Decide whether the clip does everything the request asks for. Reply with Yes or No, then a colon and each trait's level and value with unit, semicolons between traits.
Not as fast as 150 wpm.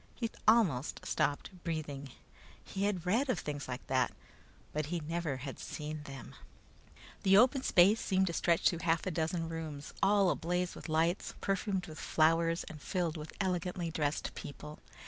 No: average, 165 wpm